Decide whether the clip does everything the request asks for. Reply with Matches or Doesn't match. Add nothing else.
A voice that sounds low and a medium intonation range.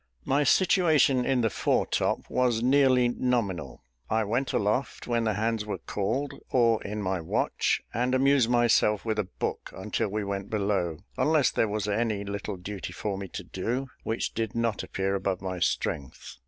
Matches